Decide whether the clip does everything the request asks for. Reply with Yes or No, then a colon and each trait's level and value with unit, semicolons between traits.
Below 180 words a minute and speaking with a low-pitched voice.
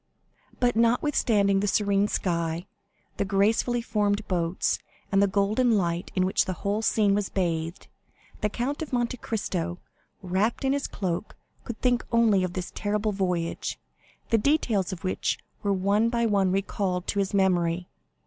No: average, 160 wpm; high, 200 Hz